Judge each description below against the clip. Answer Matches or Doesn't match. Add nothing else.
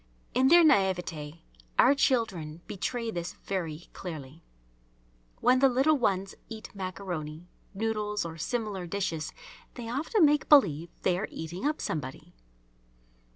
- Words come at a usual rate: Doesn't match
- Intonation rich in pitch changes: Matches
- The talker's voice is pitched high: Matches